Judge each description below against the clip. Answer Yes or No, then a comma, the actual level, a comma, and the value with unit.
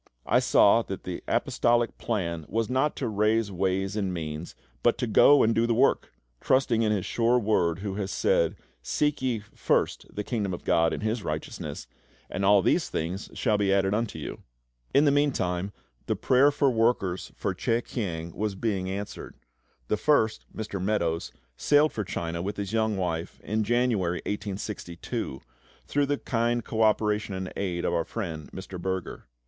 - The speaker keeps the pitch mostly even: No, average, 3.9 semitones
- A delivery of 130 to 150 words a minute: No, average, 175 wpm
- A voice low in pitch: Yes, low, 105 Hz